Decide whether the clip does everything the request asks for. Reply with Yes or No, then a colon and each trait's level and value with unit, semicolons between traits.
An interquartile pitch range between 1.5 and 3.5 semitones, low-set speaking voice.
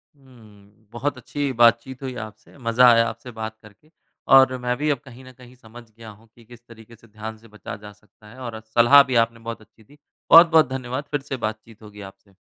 Yes: average, 2.8 semitones; low, 115 Hz